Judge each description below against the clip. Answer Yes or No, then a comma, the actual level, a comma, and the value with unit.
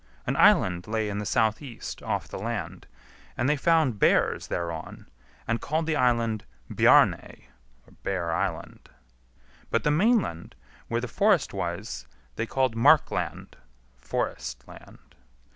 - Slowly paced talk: Yes, slow, 130 wpm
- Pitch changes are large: Yes, wide, 7.1 semitones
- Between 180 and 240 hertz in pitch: No, low, 115 Hz